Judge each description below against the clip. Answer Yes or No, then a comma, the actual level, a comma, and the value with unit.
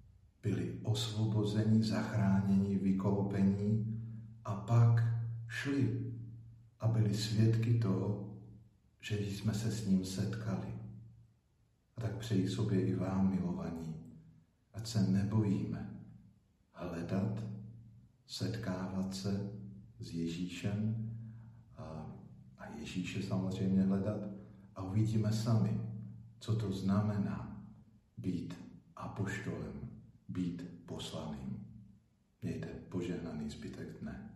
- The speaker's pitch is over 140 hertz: No, low, 105 Hz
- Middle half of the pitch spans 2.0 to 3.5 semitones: Yes, narrow, 2.6 semitones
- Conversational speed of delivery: No, slow, 90 wpm